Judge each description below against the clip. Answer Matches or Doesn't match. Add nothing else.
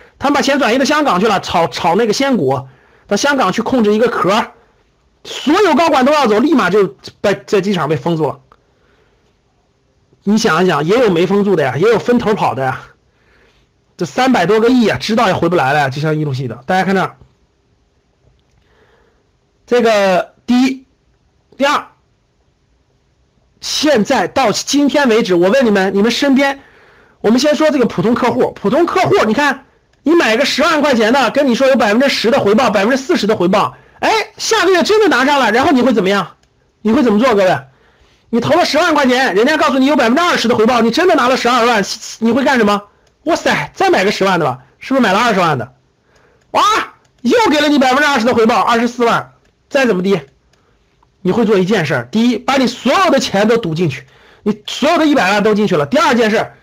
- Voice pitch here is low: Doesn't match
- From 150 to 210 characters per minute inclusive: Doesn't match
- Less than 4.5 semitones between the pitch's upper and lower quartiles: Doesn't match